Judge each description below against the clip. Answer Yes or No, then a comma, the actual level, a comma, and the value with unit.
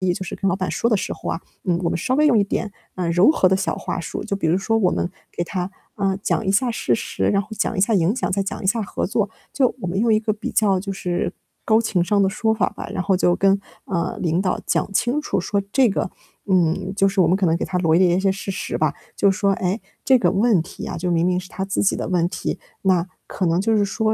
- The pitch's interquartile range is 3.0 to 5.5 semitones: No, narrow, 2.6 semitones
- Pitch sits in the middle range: No, high, 195 Hz